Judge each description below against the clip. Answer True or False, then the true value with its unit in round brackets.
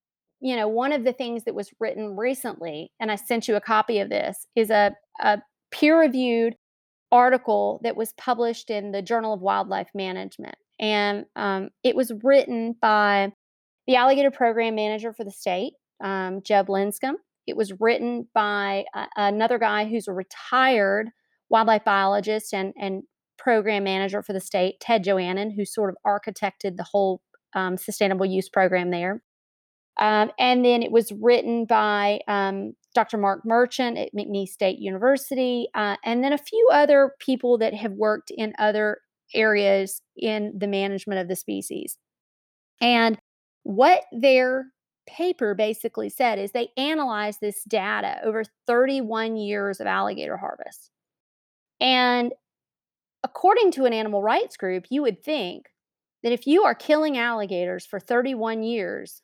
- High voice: True (220 Hz)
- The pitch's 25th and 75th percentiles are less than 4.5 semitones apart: True (3.5 semitones)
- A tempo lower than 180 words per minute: True (150 wpm)